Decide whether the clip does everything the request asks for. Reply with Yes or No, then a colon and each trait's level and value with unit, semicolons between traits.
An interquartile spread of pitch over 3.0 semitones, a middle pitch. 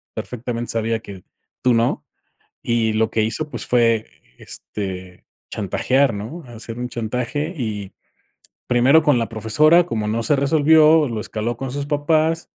No: average, 4.8 semitones; low, 120 Hz